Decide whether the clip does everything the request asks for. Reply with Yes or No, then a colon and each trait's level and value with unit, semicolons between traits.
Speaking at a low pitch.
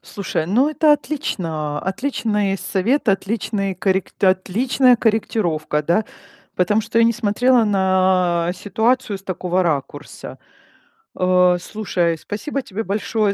No: high, 195 Hz